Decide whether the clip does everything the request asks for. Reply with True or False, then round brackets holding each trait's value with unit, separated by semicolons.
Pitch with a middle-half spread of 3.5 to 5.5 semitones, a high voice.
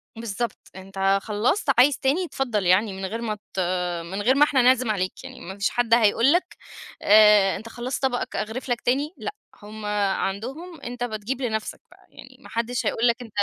True (3.8 semitones; 230 Hz)